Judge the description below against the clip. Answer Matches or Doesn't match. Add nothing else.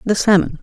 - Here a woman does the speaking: Matches